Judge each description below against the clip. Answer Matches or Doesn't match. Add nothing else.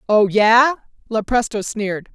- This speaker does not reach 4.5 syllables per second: Matches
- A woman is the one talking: Matches